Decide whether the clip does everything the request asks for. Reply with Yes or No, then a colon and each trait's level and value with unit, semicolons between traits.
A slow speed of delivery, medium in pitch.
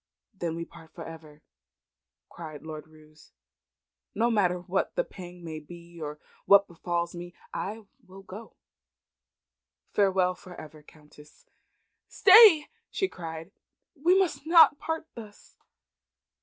Yes: slow, 125 wpm; medium, 175 Hz